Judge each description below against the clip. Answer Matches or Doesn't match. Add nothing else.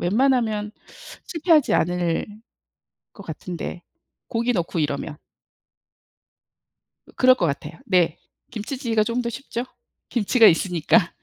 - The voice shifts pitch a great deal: Matches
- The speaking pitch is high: Matches